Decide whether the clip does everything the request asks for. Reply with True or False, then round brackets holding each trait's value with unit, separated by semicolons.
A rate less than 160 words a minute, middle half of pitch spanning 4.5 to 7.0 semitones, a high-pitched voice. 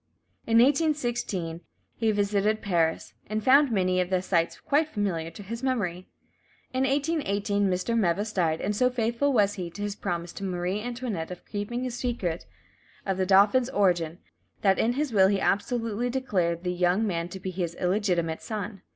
False (175 wpm; 4.8 semitones; 205 Hz)